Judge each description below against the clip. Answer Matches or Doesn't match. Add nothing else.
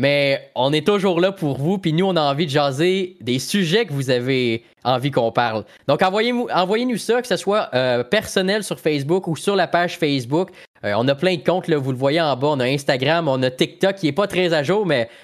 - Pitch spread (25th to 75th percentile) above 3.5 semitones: Matches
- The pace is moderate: Doesn't match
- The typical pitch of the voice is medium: Matches